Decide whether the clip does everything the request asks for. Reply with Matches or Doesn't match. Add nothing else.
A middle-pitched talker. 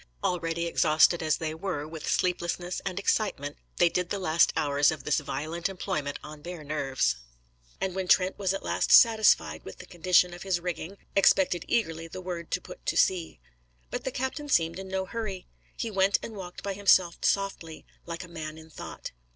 Matches